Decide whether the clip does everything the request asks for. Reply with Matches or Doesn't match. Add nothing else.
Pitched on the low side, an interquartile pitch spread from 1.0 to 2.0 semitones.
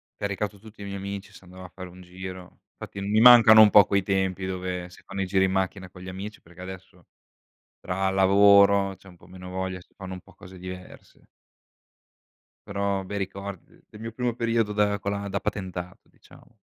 Matches